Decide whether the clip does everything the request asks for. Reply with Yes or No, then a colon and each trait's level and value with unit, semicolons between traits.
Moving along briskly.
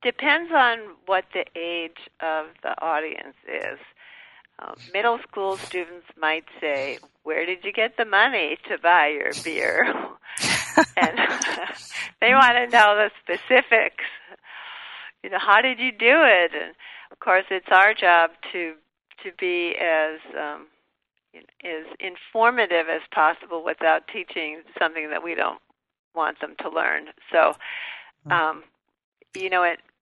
No: average, 140 wpm